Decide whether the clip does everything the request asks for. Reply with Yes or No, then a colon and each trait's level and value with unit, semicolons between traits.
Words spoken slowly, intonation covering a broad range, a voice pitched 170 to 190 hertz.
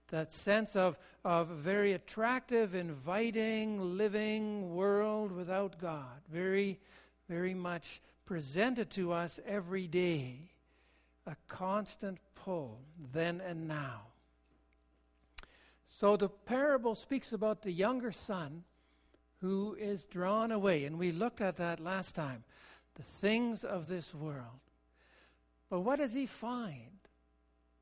Yes: slow, 115 wpm; wide, 5.7 semitones; medium, 185 Hz